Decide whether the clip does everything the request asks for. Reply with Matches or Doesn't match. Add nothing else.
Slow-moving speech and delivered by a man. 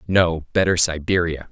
Matches